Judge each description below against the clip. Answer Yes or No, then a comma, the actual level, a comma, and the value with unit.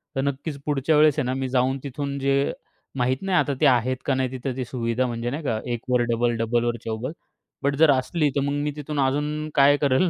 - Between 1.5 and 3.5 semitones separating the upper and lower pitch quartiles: Yes, narrow, 2.6 semitones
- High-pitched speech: No, low, 135 Hz